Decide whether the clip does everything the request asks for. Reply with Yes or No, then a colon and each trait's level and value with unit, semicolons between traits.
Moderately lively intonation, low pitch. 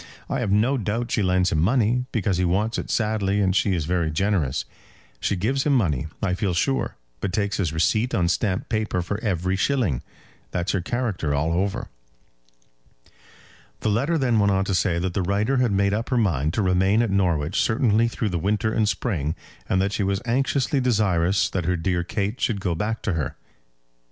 Yes: average, 3.8 semitones; low, 100 Hz